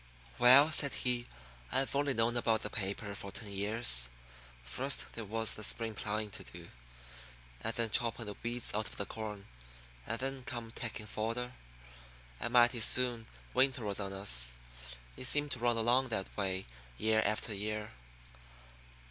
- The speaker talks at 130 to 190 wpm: Yes, average, 160 wpm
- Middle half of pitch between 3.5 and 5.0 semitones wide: No, average, 2.8 semitones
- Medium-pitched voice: No, low, 115 Hz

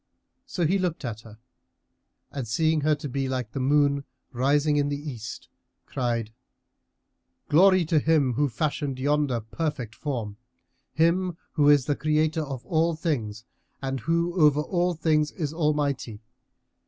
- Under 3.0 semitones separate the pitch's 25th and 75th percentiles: No, average, 3.6 semitones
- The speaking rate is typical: Yes, average, 145 wpm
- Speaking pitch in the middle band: Yes, medium, 145 Hz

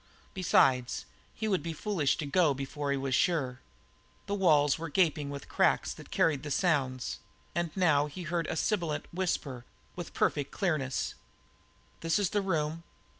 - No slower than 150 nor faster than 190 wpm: Yes, average, 165 wpm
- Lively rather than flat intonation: No, average, 3.9 semitones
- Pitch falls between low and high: Yes, medium, 155 Hz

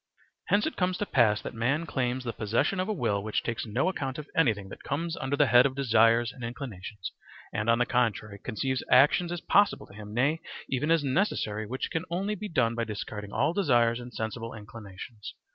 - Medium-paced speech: No, fast, 210 wpm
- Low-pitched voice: Yes, low, 125 Hz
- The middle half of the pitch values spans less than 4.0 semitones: No, average, 5.3 semitones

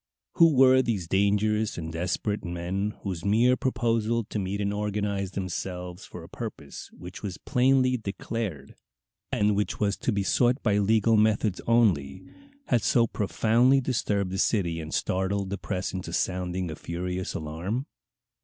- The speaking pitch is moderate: No, low, 100 Hz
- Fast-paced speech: No, average, 155 wpm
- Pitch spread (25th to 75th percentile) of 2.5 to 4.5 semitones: Yes, average, 3.8 semitones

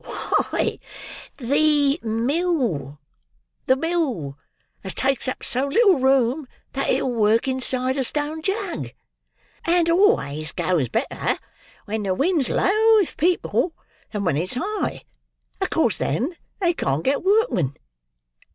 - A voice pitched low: No, very high, 265 Hz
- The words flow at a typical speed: No, slow, 120 wpm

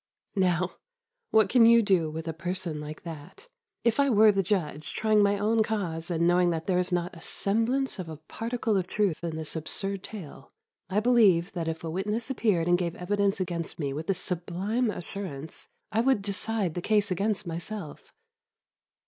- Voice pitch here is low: No, medium, 185 Hz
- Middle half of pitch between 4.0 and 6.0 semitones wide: Yes, average, 4.3 semitones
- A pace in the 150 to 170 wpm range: No, average, 180 wpm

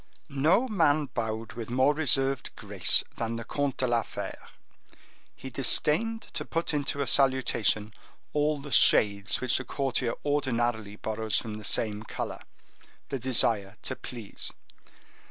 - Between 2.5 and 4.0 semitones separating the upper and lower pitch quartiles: No, average, 4.4 semitones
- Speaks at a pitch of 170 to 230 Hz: No, low, 125 Hz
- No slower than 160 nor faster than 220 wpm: No, slow, 135 wpm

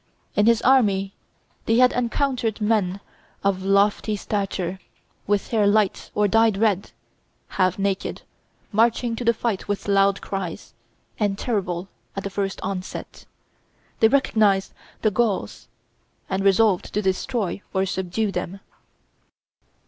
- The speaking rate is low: Yes, slow, 125 wpm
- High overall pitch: Yes, high, 200 Hz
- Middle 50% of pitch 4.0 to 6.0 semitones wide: No, narrow, 2.5 semitones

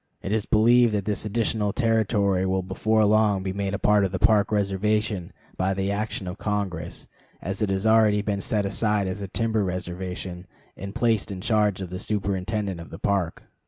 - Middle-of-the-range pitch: No, low, 100 Hz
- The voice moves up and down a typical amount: No, narrow, 2.2 semitones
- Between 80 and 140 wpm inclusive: No, average, 195 wpm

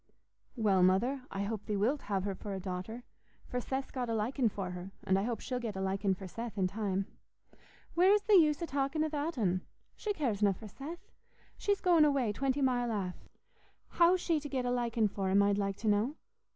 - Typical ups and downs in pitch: No, wide, 5.9 semitones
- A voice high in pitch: Yes, high, 230 Hz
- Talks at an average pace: No, fast, 210 wpm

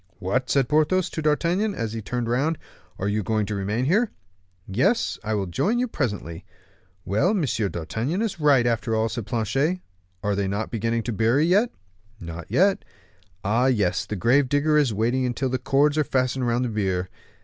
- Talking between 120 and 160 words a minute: No, average, 180 wpm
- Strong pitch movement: Yes, wide, 5.8 semitones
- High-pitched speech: No, low, 120 Hz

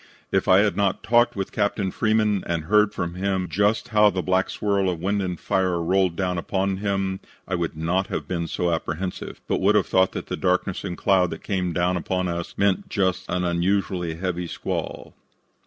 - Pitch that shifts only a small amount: Yes, narrow, 2.0 semitones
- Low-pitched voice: Yes, very low, 95 Hz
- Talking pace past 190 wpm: Yes, average, 200 wpm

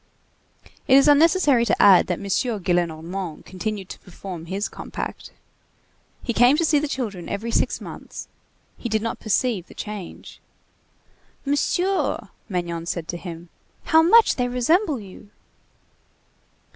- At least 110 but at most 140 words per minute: Yes, slow, 135 wpm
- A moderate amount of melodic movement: No, wide, 7.2 semitones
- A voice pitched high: Yes, high, 215 Hz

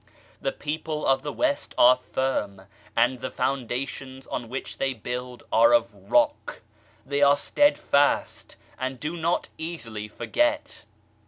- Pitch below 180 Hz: Yes, low, 135 Hz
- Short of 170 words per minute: Yes, slow, 135 wpm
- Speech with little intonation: No, average, 4.2 semitones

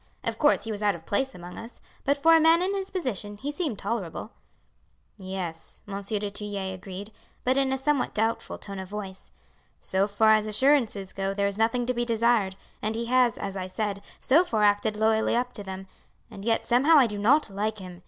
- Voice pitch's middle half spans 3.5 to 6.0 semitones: Yes, average, 4.1 semitones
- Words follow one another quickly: Yes, fast, 210 wpm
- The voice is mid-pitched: No, high, 215 Hz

